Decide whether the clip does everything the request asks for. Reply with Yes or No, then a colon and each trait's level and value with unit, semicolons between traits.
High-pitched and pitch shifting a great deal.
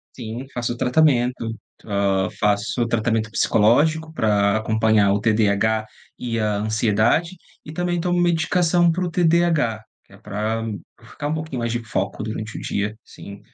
No: low, 115 Hz; wide, 6.6 semitones